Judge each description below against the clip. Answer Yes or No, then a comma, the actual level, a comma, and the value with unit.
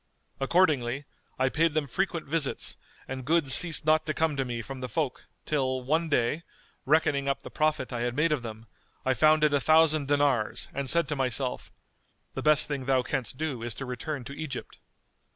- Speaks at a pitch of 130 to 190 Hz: Yes, medium, 140 Hz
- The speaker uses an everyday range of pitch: Yes, average, 3.2 semitones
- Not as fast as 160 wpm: No, average, 195 wpm